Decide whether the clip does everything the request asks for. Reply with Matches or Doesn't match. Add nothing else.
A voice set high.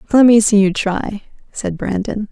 Matches